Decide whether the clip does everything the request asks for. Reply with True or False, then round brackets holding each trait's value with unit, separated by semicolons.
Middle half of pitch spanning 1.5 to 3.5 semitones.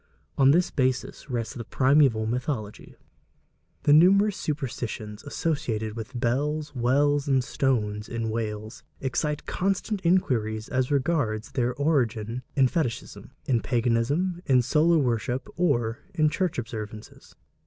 False (4.6 semitones)